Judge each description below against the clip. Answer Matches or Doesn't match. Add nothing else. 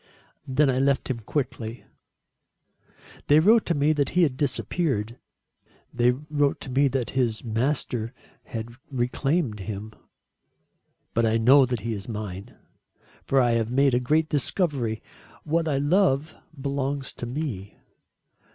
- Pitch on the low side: Matches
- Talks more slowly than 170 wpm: Matches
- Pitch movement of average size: Matches